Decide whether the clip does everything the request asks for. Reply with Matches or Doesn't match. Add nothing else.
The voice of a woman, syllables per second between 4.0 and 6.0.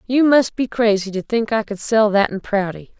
Matches